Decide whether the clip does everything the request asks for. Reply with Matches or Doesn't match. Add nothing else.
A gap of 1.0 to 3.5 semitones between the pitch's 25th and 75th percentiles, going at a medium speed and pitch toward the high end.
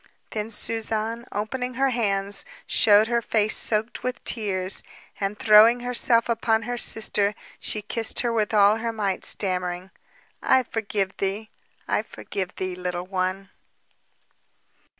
Doesn't match